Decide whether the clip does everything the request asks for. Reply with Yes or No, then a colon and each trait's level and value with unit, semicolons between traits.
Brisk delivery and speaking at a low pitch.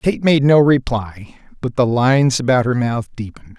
No: average, 185 wpm; low, 125 Hz